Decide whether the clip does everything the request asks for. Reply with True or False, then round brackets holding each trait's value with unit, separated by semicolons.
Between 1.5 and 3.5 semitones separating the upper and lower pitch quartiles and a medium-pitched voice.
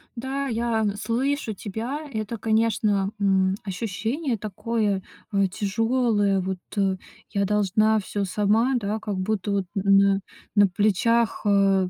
False (2.6 semitones; 210 Hz)